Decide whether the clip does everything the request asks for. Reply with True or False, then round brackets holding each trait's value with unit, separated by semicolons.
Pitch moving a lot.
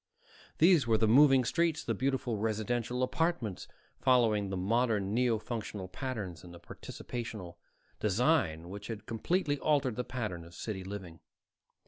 False (4.3 semitones)